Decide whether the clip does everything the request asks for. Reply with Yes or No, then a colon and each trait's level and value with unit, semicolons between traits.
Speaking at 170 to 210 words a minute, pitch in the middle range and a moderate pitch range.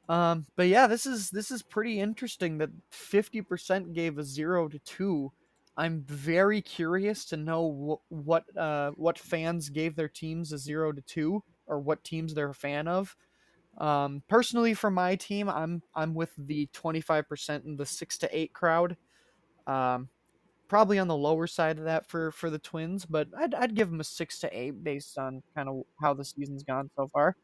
Yes: average, 200 wpm; medium, 165 Hz; average, 3.8 semitones